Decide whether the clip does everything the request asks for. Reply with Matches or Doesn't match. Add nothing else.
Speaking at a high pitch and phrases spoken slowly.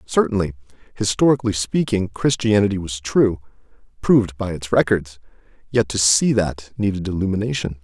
Doesn't match